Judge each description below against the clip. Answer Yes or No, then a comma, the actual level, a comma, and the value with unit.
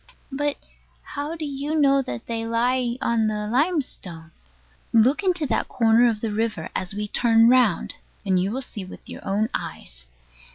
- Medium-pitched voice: No, high, 230 Hz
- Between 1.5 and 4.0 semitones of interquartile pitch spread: No, average, 4.5 semitones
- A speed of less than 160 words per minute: No, average, 170 wpm